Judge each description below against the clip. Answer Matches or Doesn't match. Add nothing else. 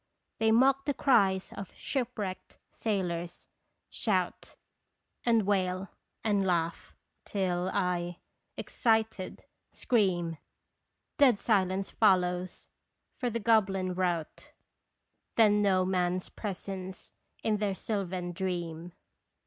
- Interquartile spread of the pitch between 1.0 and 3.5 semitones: Matches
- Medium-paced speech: Doesn't match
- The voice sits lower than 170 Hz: Doesn't match